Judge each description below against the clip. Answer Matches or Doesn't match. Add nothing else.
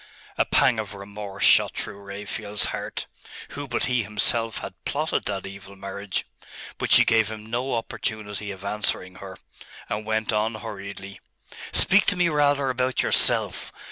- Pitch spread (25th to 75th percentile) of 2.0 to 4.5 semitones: Matches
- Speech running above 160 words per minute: Doesn't match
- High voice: Doesn't match